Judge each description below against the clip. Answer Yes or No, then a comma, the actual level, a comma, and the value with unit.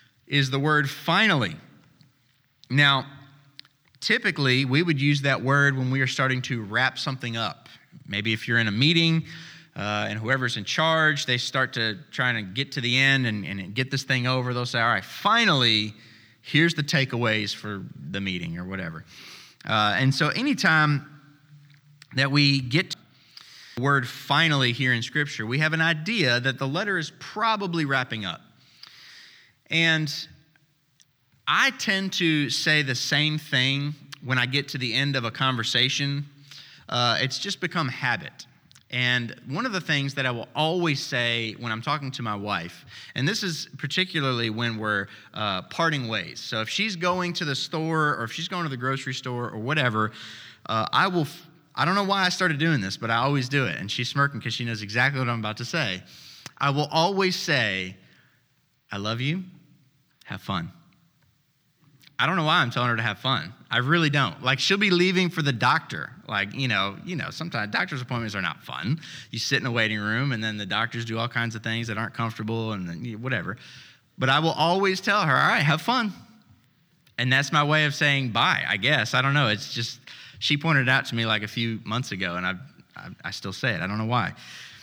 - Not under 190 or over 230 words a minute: Yes, average, 200 wpm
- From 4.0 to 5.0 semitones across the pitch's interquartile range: Yes, average, 4.7 semitones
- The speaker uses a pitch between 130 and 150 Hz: Yes, low, 135 Hz